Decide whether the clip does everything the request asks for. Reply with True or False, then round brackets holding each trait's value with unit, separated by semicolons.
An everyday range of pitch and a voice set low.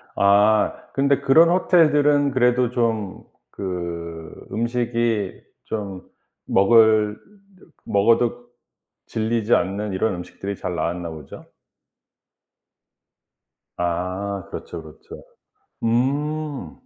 True (4.6 semitones; 110 Hz)